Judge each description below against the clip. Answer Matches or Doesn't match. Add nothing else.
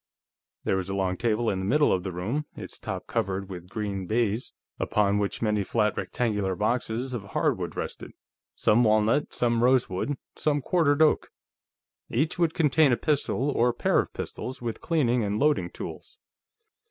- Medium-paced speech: Matches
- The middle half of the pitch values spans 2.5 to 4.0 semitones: Doesn't match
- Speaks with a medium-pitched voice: Doesn't match